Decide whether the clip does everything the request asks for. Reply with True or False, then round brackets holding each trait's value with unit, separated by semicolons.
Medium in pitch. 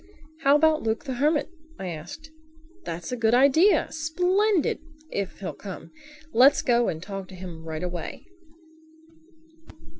False (250 Hz)